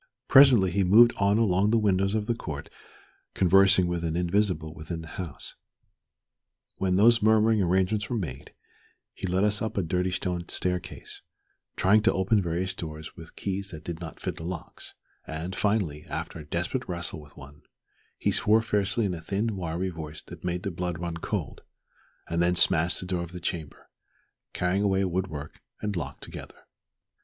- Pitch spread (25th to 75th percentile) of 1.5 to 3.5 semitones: Yes, average, 3.2 semitones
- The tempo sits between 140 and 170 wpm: No, average, 180 wpm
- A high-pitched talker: No, very low, 90 Hz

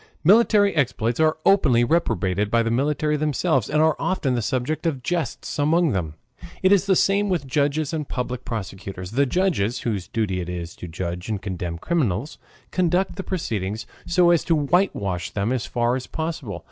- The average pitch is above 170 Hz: No, low, 130 Hz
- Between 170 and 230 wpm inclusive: Yes, average, 180 wpm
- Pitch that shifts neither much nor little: No, wide, 8.1 semitones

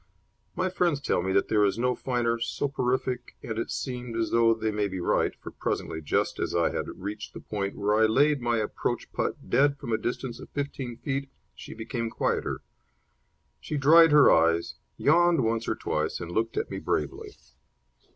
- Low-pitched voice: Yes, low, 115 Hz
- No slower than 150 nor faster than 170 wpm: No, average, 190 wpm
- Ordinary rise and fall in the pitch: Yes, average, 4.1 semitones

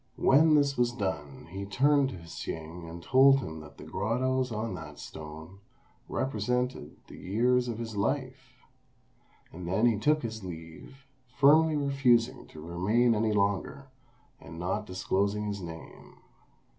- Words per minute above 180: No, average, 145 wpm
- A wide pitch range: Yes, wide, 6.6 semitones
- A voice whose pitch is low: Yes, low, 110 Hz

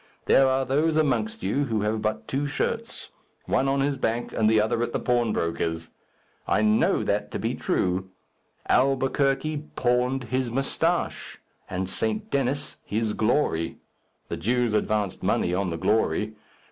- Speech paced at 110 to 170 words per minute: Yes, average, 150 wpm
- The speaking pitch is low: Yes, low, 120 Hz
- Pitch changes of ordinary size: Yes, average, 4.3 semitones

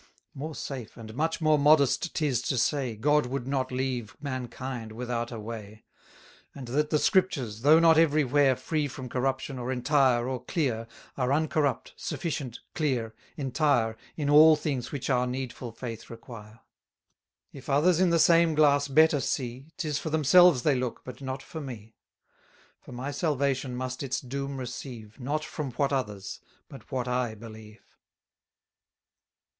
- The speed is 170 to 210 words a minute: No, average, 160 wpm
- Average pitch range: Yes, average, 3.4 semitones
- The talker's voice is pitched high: No, low, 130 Hz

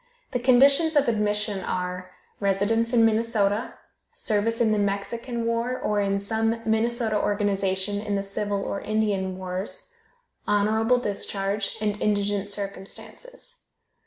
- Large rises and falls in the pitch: No, narrow, 2.5 semitones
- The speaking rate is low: Yes, slow, 125 wpm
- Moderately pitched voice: No, high, 210 Hz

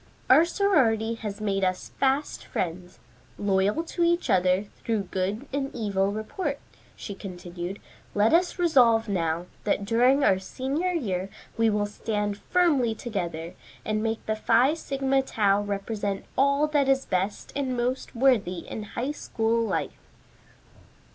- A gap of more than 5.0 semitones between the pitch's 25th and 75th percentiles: Yes, wide, 5.4 semitones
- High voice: Yes, high, 220 Hz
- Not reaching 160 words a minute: Yes, average, 140 wpm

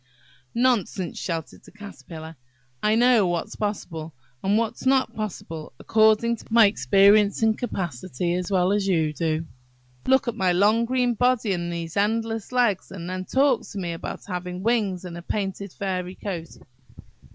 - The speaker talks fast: No, average, 160 wpm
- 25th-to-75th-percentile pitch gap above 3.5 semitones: Yes, average, 4.2 semitones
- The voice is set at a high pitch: Yes, high, 200 Hz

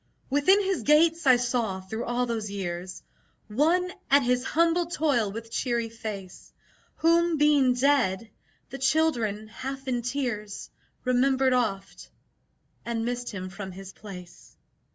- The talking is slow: Yes, slow, 130 wpm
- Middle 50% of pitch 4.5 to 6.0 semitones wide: Yes, average, 5.2 semitones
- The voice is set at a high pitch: Yes, high, 245 Hz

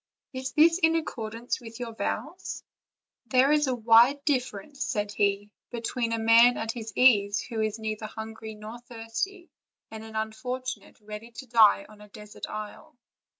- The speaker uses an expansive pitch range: No, average, 2.9 semitones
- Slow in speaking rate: No, average, 160 wpm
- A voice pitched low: No, high, 225 Hz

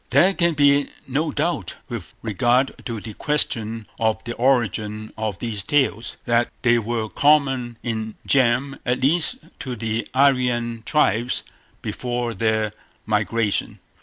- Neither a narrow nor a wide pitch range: Yes, average, 3.6 semitones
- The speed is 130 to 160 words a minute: Yes, slow, 135 wpm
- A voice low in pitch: Yes, low, 120 Hz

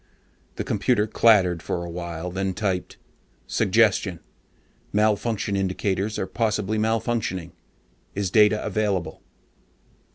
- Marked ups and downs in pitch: No, average, 2.9 semitones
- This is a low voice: Yes, low, 100 Hz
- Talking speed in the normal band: No, slow, 95 wpm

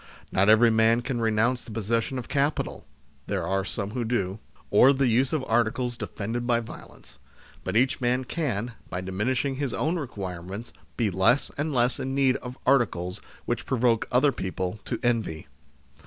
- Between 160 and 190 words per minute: Yes, average, 170 wpm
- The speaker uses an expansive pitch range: No, average, 3.5 semitones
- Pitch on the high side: No, low, 120 Hz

